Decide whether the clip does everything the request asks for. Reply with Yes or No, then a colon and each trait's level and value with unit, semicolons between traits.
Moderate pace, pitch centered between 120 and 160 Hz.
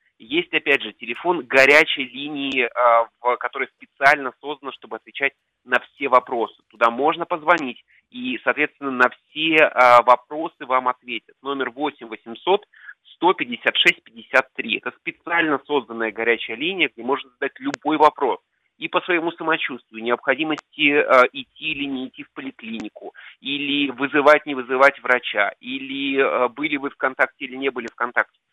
Yes: average, 135 wpm; medium, 140 Hz